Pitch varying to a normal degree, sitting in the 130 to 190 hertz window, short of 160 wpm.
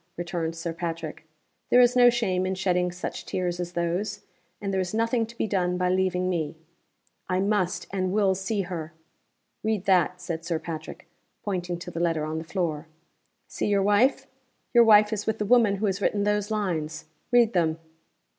No: average, 3.3 semitones; medium, 185 Hz; average, 185 wpm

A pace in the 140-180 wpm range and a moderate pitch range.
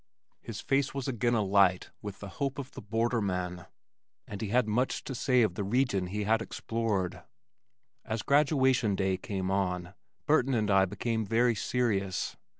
Yes: average, 160 wpm; average, 4.2 semitones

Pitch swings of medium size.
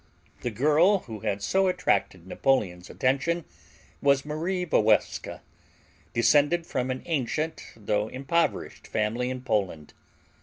No: wide, 6.7 semitones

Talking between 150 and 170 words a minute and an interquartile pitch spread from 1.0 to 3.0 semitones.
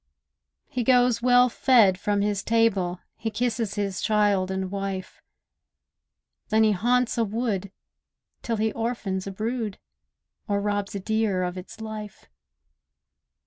No: slow, 135 wpm; average, 2.7 semitones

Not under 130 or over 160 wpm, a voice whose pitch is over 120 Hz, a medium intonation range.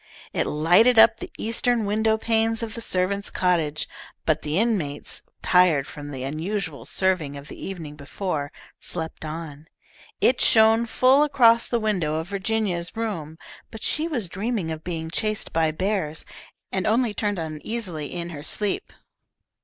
No: average, 155 wpm; medium, 185 Hz; wide, 5.8 semitones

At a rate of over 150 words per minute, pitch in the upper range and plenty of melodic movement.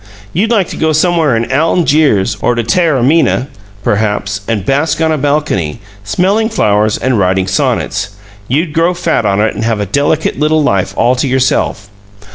No: average, 170 wpm; low, 135 Hz; wide, 7.1 semitones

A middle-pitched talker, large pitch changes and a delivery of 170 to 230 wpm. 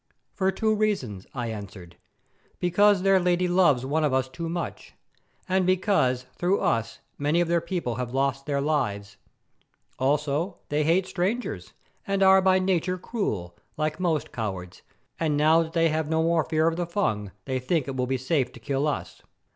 Yes: medium, 155 Hz; wide, 5.7 semitones; average, 180 wpm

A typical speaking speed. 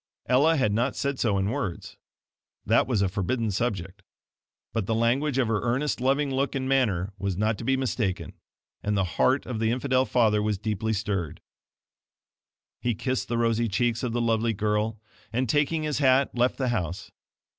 Yes: average, 180 wpm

